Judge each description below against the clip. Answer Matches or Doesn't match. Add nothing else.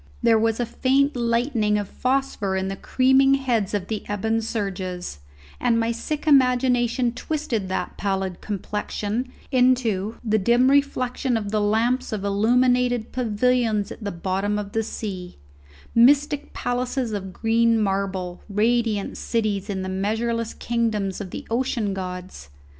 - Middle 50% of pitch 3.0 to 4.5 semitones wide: Matches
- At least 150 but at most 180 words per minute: Doesn't match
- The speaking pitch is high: Matches